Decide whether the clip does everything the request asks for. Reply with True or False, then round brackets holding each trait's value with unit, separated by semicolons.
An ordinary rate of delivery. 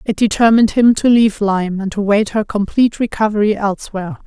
True (170 wpm)